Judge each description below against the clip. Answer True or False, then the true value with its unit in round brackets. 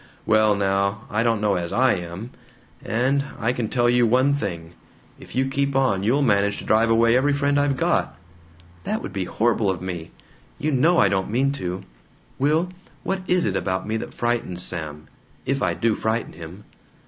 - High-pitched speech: False (115 Hz)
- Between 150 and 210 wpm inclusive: True (190 wpm)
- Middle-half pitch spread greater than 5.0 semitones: True (5.6 semitones)